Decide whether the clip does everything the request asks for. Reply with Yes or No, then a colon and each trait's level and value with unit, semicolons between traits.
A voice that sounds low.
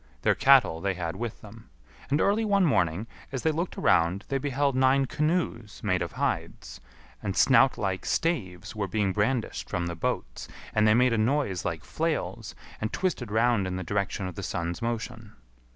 Yes: low, 110 Hz